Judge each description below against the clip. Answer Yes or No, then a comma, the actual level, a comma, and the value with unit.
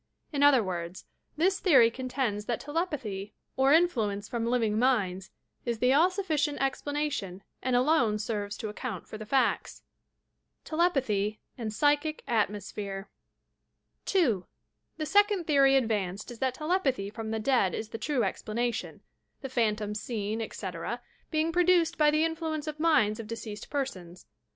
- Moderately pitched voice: No, high, 245 Hz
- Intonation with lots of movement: Yes, wide, 6.1 semitones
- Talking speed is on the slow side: No, average, 150 wpm